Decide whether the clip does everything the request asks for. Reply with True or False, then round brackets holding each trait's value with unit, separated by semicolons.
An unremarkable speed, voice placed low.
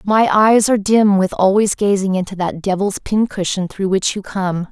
False (190 wpm; 195 Hz)